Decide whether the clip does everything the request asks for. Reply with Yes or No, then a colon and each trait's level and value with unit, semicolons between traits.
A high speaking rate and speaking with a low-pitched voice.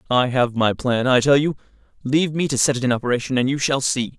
Yes: fast, 260 wpm; low, 130 Hz